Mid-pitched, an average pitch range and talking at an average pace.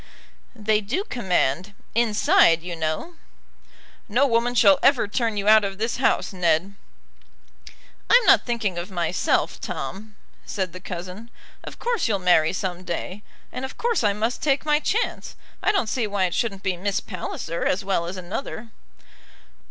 No: high, 205 Hz; average, 4.7 semitones; average, 160 wpm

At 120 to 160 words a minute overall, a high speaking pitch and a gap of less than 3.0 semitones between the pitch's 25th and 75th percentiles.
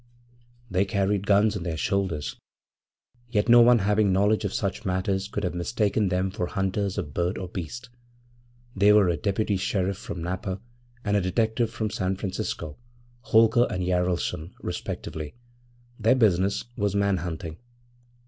No: average, 150 wpm; low, 100 Hz; narrow, 2.5 semitones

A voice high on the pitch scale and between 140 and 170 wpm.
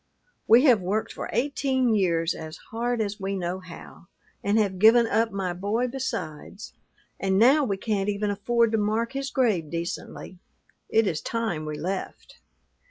Yes: high, 205 Hz; average, 165 wpm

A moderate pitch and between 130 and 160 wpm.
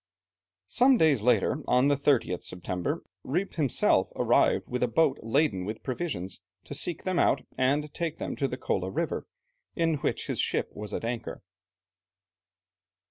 No: low, 130 Hz; average, 155 wpm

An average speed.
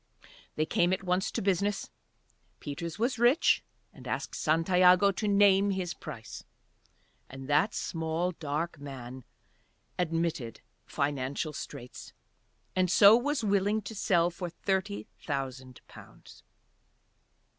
No: slow, 115 wpm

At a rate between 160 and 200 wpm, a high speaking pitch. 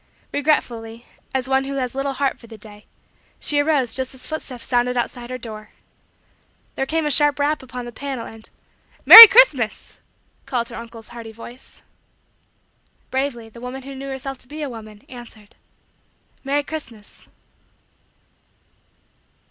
No: average, 150 wpm; very high, 255 Hz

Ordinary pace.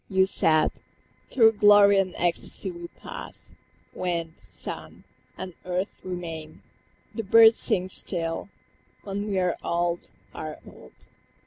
No: slow, 120 wpm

